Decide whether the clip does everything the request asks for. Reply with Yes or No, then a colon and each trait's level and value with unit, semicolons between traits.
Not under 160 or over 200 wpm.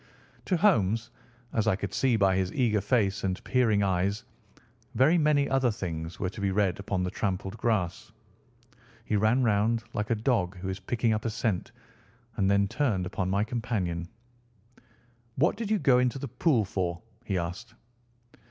Yes: average, 170 wpm